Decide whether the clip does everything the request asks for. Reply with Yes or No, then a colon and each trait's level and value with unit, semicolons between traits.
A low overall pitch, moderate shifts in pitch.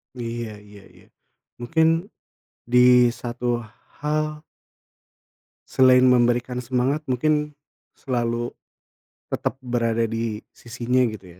No: low, 120 Hz; narrow, 1.8 semitones